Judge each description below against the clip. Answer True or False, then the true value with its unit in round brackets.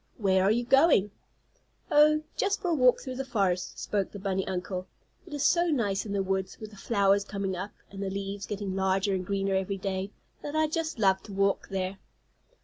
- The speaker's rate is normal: False (210 wpm)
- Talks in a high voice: True (200 Hz)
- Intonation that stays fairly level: False (4.1 semitones)